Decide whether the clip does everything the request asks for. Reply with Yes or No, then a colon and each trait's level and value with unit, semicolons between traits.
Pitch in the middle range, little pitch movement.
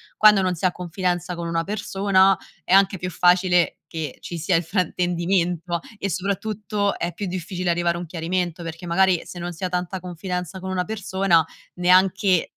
Yes: medium, 180 Hz; narrow, 1.7 semitones